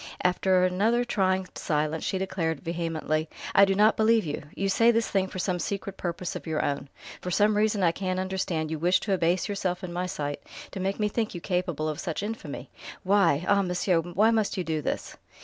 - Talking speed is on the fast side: Yes, fast, 210 wpm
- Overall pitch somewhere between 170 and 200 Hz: Yes, medium, 185 Hz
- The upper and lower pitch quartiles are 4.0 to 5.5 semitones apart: No, average, 3.1 semitones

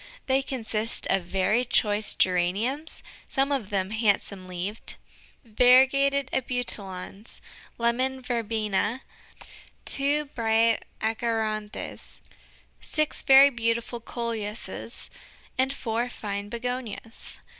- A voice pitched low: No, high, 230 Hz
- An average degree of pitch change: Yes, average, 3.7 semitones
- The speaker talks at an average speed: No, slow, 90 wpm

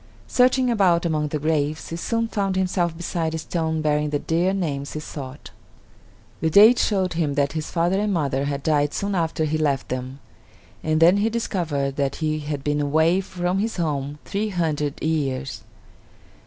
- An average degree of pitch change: Yes, average, 3.9 semitones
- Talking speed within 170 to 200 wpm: Yes, average, 180 wpm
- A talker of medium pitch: Yes, medium, 160 Hz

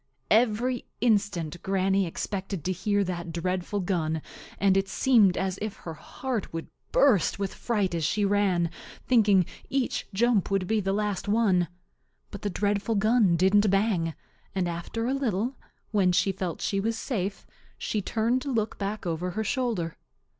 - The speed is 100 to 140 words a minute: No, average, 160 wpm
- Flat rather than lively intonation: No, average, 3.2 semitones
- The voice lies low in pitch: No, high, 200 Hz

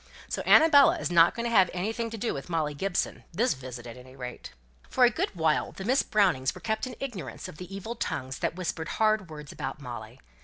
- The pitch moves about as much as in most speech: No, wide, 8.6 semitones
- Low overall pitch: No, medium, 180 Hz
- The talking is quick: Yes, fast, 220 wpm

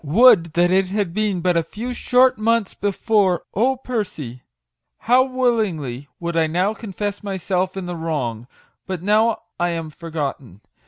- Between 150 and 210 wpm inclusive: Yes, average, 160 wpm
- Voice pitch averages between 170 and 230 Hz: Yes, medium, 185 Hz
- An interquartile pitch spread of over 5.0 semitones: No, average, 4.7 semitones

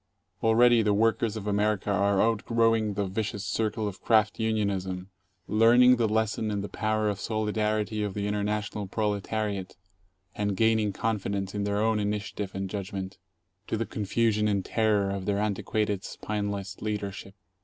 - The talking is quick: No, average, 155 wpm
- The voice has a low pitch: Yes, low, 105 Hz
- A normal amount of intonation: No, narrow, 1.6 semitones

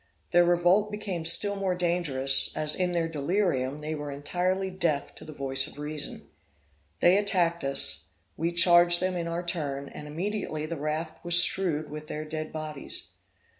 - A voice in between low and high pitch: Yes, medium, 165 Hz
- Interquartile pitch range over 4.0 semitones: No, average, 3.0 semitones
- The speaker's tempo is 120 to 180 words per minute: Yes, average, 170 wpm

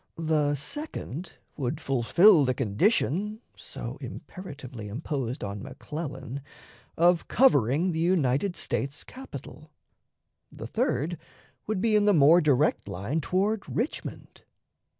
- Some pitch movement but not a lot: No, wide, 5.9 semitones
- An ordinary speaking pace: No, slow, 110 wpm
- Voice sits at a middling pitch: Yes, medium, 155 Hz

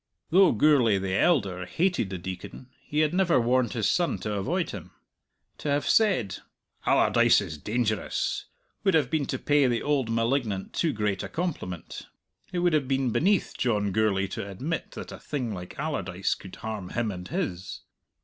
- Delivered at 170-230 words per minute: Yes, average, 175 wpm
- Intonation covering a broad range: Yes, wide, 7.5 semitones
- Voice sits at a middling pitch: No, low, 120 Hz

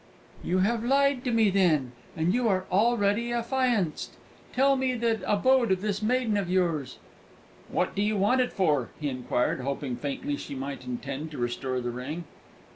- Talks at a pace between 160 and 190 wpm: Yes, average, 175 wpm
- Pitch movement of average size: No, wide, 8.9 semitones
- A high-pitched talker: Yes, high, 195 Hz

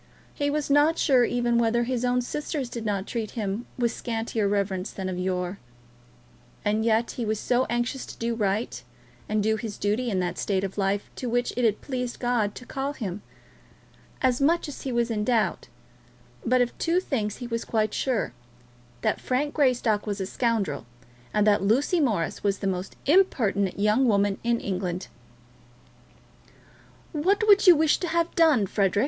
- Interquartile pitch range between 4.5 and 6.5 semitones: No, average, 4.1 semitones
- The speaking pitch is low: No, high, 230 Hz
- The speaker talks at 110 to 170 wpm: No, average, 180 wpm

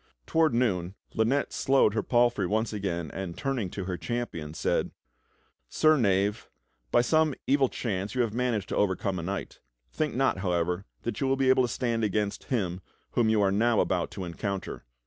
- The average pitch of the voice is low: Yes, low, 110 Hz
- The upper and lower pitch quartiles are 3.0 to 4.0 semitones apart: No, average, 4.8 semitones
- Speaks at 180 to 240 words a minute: Yes, average, 185 wpm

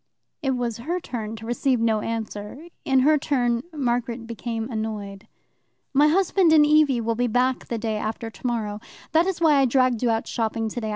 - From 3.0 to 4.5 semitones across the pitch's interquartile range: Yes, average, 3.6 semitones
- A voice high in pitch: Yes, high, 240 Hz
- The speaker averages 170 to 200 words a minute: Yes, average, 185 wpm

